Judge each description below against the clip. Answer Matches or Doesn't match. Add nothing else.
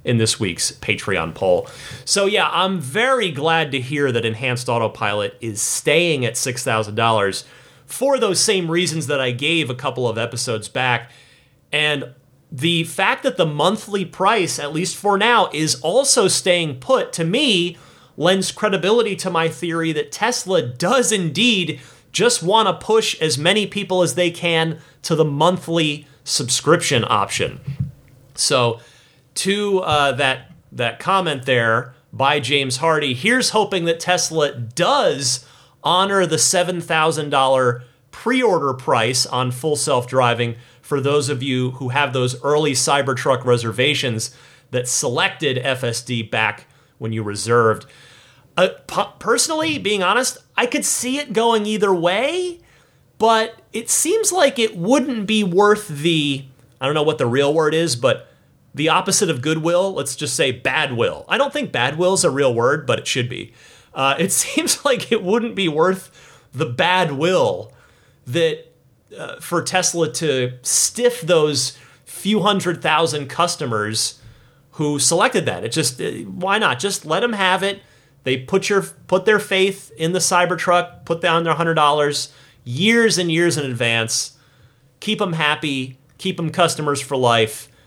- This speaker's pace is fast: Doesn't match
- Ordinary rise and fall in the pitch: Doesn't match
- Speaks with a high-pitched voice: Doesn't match